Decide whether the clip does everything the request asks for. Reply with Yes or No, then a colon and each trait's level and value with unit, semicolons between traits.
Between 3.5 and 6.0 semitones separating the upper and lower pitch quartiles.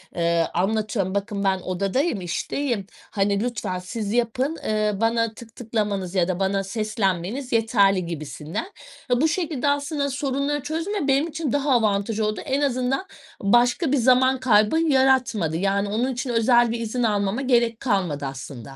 Yes: average, 5.0 semitones